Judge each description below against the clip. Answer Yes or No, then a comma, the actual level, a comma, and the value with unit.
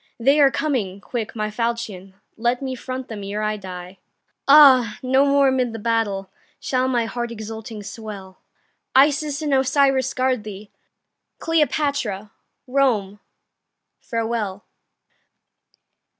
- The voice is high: Yes, high, 235 Hz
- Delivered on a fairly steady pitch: No, average, 4.2 semitones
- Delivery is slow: Yes, slow, 120 wpm